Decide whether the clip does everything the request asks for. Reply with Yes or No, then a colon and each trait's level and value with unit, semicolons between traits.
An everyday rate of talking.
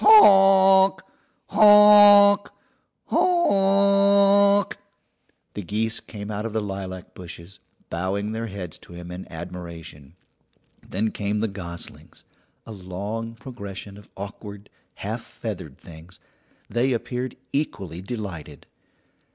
No: slow, 105 wpm